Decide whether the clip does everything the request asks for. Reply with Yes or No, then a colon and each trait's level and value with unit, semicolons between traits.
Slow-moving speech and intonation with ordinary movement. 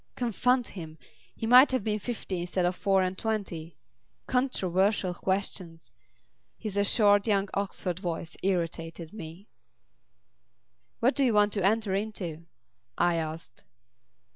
Yes: slow, 125 wpm; average, 3.8 semitones